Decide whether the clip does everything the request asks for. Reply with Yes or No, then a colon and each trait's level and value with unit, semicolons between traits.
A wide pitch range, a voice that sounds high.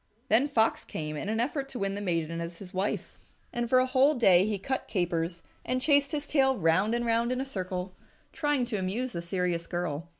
Yes: wide, 6.4 semitones; high, 210 Hz